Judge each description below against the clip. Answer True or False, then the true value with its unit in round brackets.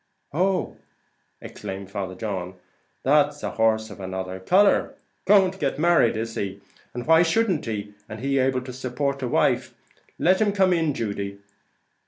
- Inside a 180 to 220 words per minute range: False (160 wpm)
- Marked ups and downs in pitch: True (8.8 semitones)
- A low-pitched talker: True (125 Hz)